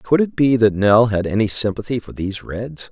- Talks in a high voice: No, low, 110 Hz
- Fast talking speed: Yes, fast, 225 wpm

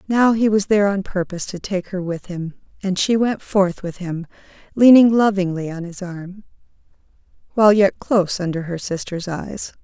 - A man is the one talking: No, female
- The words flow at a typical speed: Yes, average, 175 wpm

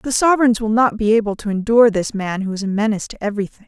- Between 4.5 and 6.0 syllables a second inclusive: No, 7.2 syllables/s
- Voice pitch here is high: Yes, high, 215 Hz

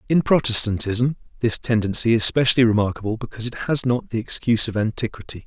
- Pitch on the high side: No, low, 115 Hz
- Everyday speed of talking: Yes, average, 165 wpm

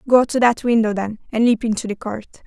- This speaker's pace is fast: Yes, fast, 245 wpm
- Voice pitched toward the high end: Yes, high, 225 Hz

